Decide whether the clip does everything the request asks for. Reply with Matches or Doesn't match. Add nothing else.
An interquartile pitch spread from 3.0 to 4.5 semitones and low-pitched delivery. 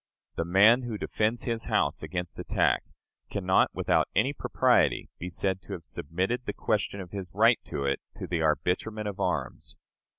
Matches